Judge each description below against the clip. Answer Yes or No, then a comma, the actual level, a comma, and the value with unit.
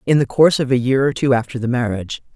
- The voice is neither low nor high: No, low, 130 Hz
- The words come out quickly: Yes, fast, 280 wpm